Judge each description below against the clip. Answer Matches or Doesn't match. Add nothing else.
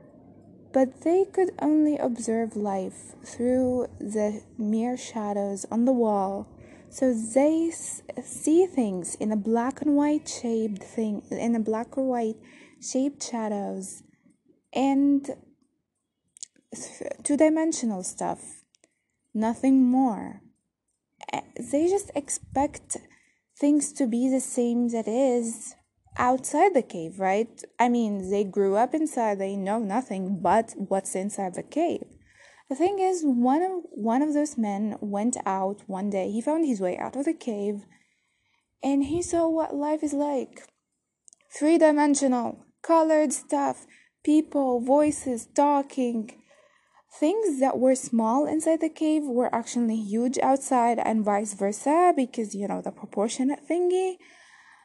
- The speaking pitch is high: Matches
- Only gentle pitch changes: Doesn't match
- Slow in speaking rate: Matches